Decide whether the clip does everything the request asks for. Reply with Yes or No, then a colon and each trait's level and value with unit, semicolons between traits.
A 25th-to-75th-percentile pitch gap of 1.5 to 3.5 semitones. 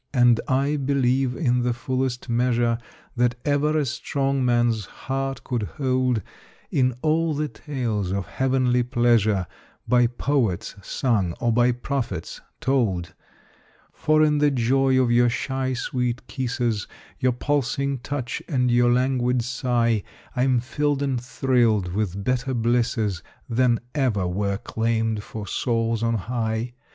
Yes: narrow, 2.4 semitones